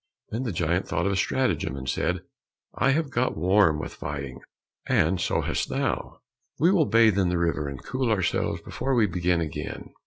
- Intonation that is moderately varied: No, wide, 6.9 semitones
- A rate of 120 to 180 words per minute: No, average, 190 wpm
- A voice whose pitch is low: Yes, very low, 90 Hz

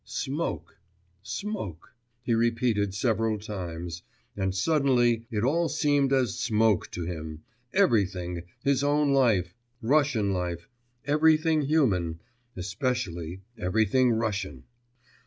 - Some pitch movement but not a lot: No, wide, 7.0 semitones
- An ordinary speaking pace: No, slow, 100 wpm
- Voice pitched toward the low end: Yes, low, 110 Hz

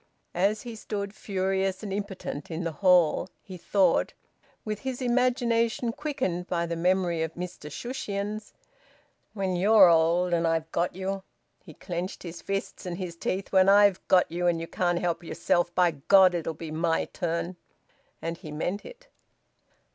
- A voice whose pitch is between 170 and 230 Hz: Yes, medium, 185 Hz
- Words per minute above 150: Yes, average, 160 wpm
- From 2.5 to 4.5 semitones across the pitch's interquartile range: Yes, average, 2.9 semitones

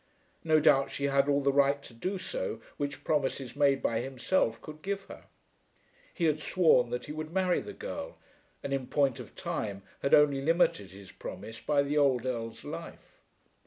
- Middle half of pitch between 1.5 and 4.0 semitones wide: Yes, average, 3.5 semitones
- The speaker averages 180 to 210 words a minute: Yes, average, 185 wpm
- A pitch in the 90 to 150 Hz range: Yes, medium, 140 Hz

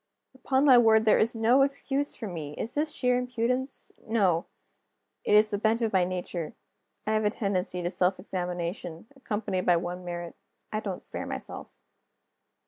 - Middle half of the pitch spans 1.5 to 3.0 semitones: No, average, 5.0 semitones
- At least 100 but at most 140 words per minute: No, average, 170 wpm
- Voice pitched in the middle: No, high, 210 Hz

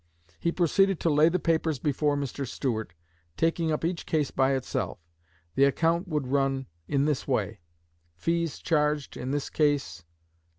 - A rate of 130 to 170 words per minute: Yes, average, 155 wpm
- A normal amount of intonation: Yes, average, 3.3 semitones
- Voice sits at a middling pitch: Yes, medium, 150 Hz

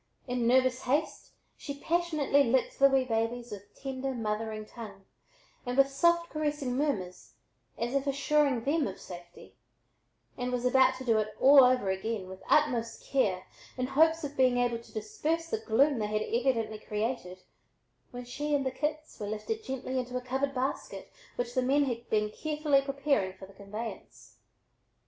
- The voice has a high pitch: Yes, very high, 255 Hz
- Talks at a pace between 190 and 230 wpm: No, average, 170 wpm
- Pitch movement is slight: No, average, 4.0 semitones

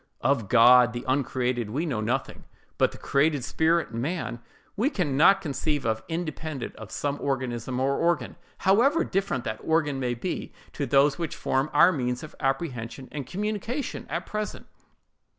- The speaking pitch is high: No, medium, 140 Hz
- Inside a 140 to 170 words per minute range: Yes, average, 160 wpm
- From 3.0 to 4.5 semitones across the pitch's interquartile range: No, average, 5.1 semitones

